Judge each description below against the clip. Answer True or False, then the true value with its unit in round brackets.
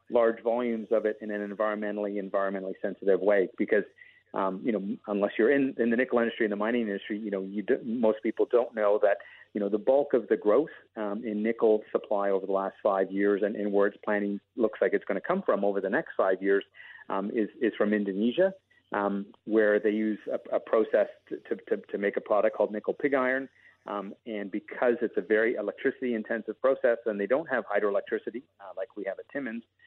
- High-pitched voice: False (105 Hz)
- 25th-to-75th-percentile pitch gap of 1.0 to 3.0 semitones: True (2.5 semitones)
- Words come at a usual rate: False (220 wpm)